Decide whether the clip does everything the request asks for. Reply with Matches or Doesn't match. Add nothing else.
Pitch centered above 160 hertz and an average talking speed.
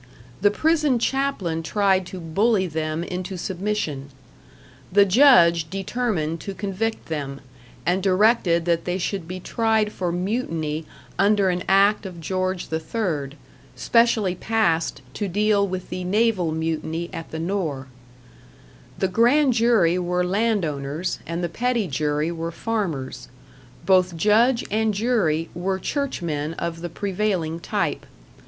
Doesn't match